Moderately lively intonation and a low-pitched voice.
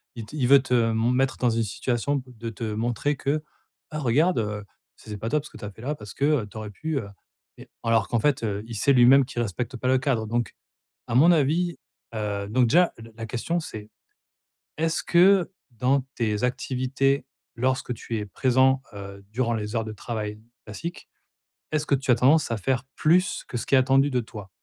Yes: average, 3.9 semitones; low, 125 Hz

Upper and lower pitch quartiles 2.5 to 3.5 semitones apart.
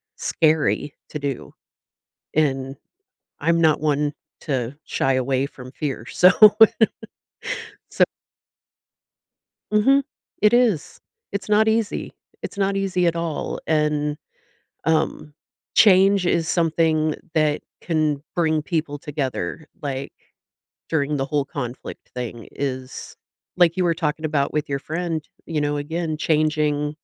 Yes: average, 2.8 semitones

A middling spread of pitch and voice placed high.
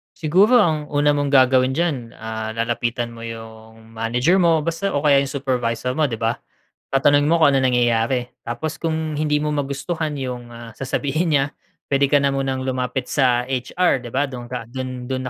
No: average, 3.6 semitones; low, 130 Hz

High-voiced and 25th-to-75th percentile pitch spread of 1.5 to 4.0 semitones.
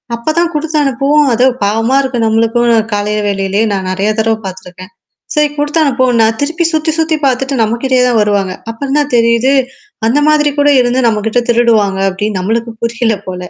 No: high, 235 Hz; average, 4.6 semitones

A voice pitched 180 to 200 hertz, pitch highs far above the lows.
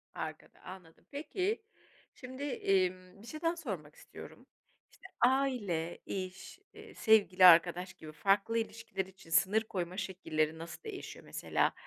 Yes: high, 190 Hz; wide, 5.9 semitones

